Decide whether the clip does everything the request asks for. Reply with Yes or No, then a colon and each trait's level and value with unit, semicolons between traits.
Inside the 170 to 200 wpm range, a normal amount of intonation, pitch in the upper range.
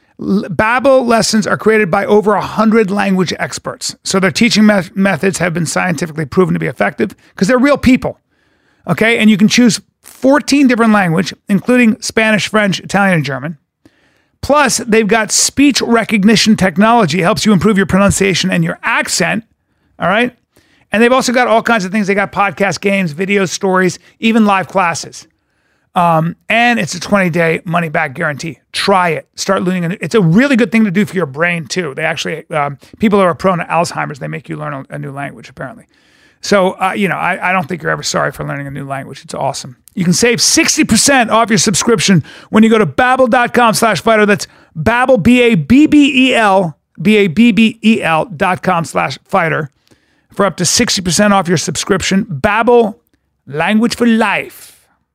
Yes: average, 180 wpm; average, 4.1 semitones; high, 200 Hz